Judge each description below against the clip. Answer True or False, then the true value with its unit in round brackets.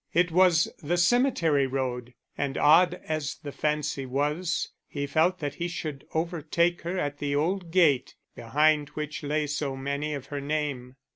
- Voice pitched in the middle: True (150 Hz)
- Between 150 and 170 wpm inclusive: True (160 wpm)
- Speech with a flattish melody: False (3.2 semitones)